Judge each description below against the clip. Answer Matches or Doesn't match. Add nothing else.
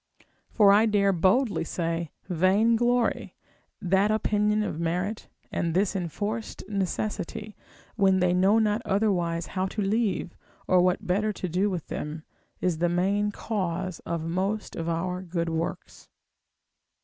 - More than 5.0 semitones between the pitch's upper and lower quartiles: Doesn't match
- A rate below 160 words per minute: Matches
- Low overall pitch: Doesn't match